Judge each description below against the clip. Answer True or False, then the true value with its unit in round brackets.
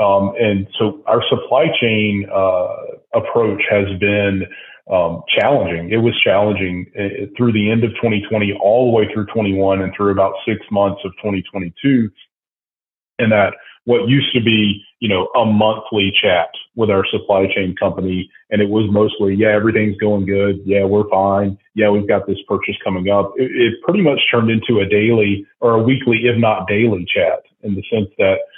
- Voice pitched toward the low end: True (105 Hz)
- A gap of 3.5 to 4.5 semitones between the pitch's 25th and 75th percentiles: False (2.4 semitones)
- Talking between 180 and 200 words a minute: True (185 wpm)